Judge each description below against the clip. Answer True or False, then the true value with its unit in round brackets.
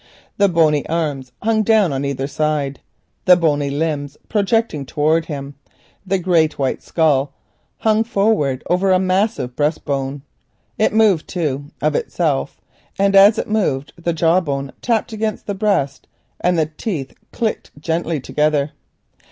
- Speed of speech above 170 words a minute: False (145 wpm)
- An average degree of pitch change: False (5.7 semitones)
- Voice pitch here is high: False (165 Hz)